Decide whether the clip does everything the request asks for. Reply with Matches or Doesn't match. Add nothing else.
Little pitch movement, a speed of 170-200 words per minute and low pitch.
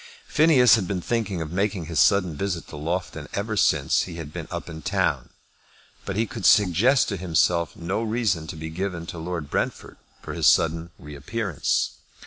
Doesn't match